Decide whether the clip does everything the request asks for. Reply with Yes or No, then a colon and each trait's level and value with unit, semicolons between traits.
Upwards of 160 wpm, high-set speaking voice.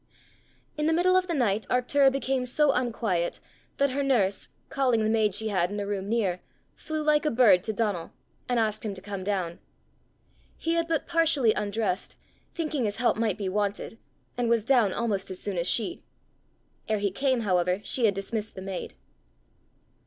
Yes: average, 185 wpm; high, 220 Hz